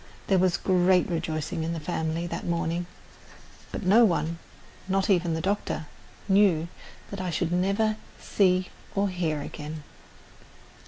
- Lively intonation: No, average, 2.8 semitones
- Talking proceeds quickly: No, average, 140 wpm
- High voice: No, medium, 175 Hz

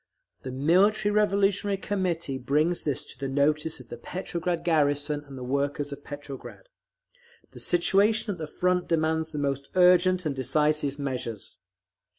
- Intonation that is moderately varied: Yes, average, 4.3 semitones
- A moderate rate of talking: Yes, average, 150 wpm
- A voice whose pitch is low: No, medium, 155 Hz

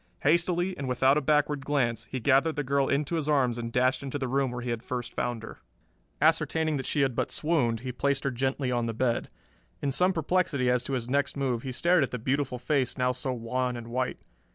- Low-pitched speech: Yes, low, 130 Hz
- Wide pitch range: No, narrow, 2.6 semitones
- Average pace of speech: No, fast, 230 wpm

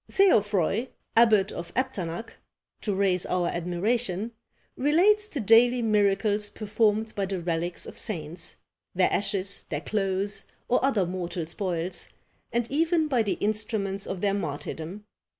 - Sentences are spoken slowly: Yes, slow, 130 wpm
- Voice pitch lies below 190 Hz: No, high, 200 Hz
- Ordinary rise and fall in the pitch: Yes, average, 3.9 semitones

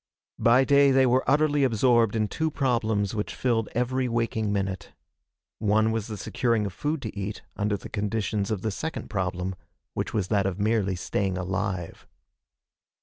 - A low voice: Yes, low, 110 Hz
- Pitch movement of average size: Yes, average, 3.7 semitones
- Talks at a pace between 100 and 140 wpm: No, average, 165 wpm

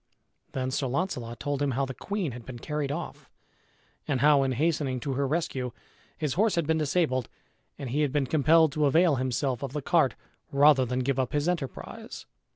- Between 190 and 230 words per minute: Yes, average, 195 wpm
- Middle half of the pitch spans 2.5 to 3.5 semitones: Yes, average, 3.1 semitones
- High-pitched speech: No, medium, 140 Hz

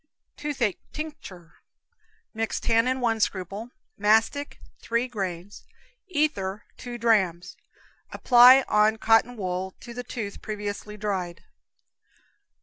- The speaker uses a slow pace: Yes, slow, 100 wpm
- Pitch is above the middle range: Yes, high, 220 Hz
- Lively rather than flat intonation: No, average, 4.0 semitones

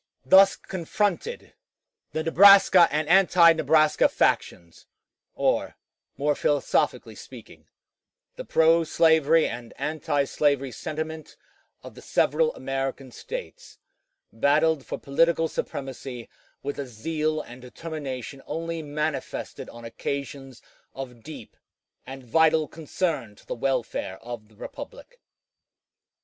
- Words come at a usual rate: No, slow, 110 wpm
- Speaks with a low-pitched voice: No, medium, 150 Hz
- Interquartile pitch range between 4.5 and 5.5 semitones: No, average, 3.5 semitones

